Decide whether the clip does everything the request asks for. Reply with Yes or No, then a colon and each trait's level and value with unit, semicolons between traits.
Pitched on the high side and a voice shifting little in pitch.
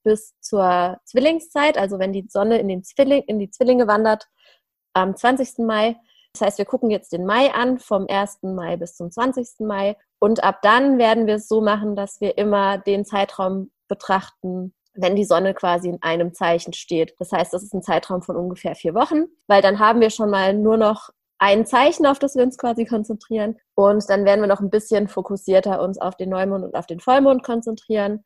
No: high, 205 Hz; average, 3.0 semitones